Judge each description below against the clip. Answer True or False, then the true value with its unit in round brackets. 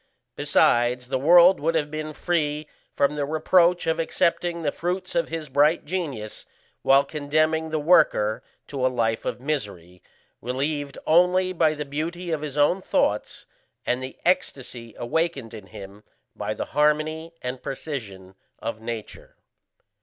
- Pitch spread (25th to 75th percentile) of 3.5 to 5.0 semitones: True (4.6 semitones)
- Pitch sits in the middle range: True (150 Hz)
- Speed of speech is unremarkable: True (145 wpm)